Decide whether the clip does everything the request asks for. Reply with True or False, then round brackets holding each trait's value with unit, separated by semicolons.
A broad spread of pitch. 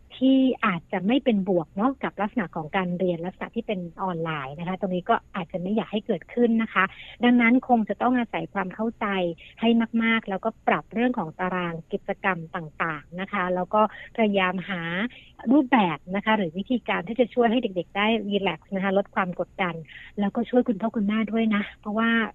False (3.9 semitones)